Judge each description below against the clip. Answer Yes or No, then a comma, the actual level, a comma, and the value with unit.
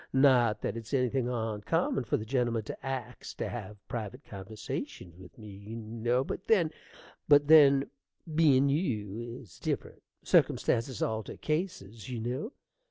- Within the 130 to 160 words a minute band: Yes, average, 145 wpm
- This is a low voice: Yes, low, 120 Hz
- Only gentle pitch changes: No, average, 4.1 semitones